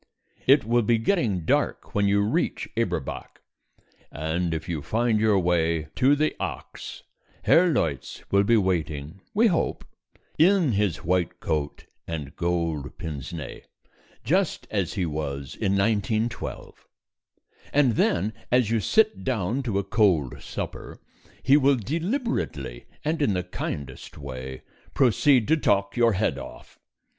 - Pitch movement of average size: No, wide, 7.3 semitones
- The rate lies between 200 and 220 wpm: No, average, 140 wpm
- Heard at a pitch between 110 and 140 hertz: No, low, 100 Hz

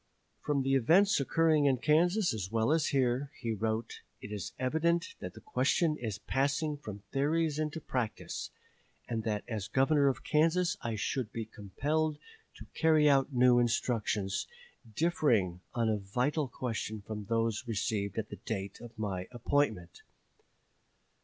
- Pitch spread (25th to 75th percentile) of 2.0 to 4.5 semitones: No, wide, 5.6 semitones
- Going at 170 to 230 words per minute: No, average, 150 wpm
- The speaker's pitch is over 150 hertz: No, low, 125 Hz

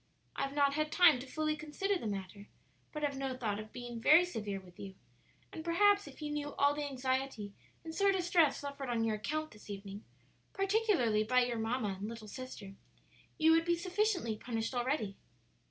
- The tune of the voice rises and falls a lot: Yes, wide, 6.1 semitones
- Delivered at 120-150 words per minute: No, average, 190 wpm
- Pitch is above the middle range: Yes, very high, 270 Hz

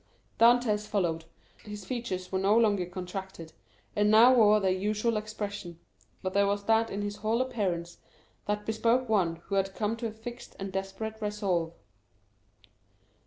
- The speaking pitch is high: Yes, high, 205 Hz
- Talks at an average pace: Yes, average, 160 wpm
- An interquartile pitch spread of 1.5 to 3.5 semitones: Yes, narrow, 2.6 semitones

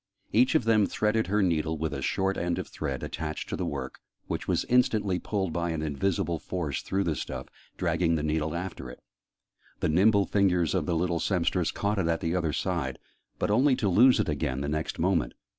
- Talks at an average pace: No, fast, 210 wpm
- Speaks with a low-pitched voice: Yes, very low, 85 Hz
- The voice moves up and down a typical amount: Yes, average, 4.1 semitones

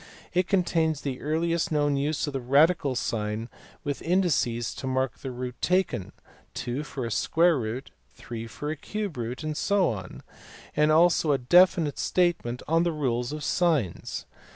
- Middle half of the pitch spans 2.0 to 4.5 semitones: No, average, 5.3 semitones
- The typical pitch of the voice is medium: Yes, medium, 145 Hz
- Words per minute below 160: No, average, 165 wpm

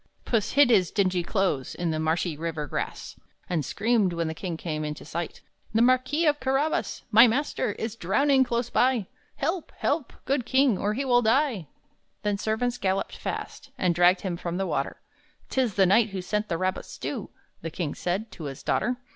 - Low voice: No, high, 205 Hz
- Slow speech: No, average, 190 wpm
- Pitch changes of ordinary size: No, wide, 6.2 semitones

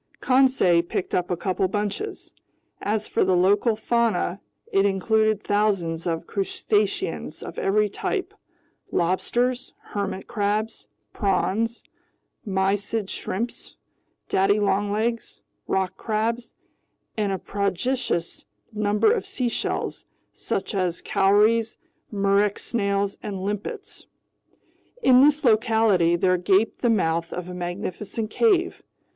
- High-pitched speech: Yes, high, 205 Hz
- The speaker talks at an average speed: No, slow, 105 wpm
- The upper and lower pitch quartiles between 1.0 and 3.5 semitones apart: Yes, average, 3.0 semitones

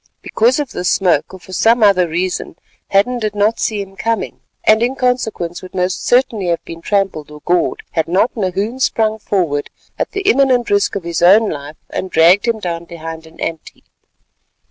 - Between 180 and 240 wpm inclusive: Yes, average, 190 wpm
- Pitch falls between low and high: No, high, 195 Hz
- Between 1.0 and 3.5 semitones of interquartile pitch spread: No, average, 4.7 semitones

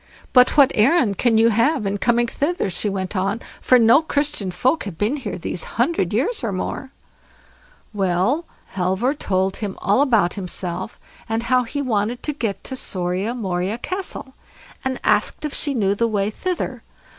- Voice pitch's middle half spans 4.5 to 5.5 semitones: Yes, average, 5.2 semitones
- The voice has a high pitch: Yes, high, 225 Hz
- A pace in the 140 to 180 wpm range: Yes, average, 170 wpm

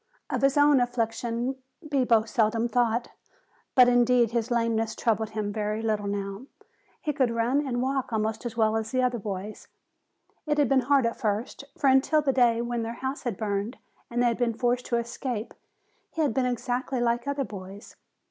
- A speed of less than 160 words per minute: No, average, 185 wpm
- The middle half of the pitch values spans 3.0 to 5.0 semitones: No, narrow, 2.6 semitones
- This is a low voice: No, high, 235 Hz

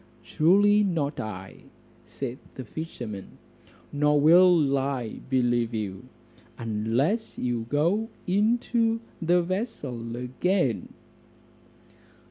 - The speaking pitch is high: No, medium, 145 Hz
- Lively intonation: Yes, wide, 7.6 semitones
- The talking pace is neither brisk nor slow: No, slow, 90 wpm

